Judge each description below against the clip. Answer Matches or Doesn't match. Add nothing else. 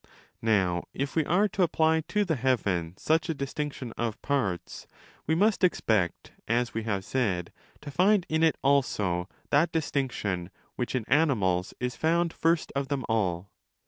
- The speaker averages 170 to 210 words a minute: Doesn't match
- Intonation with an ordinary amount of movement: Doesn't match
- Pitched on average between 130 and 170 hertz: Matches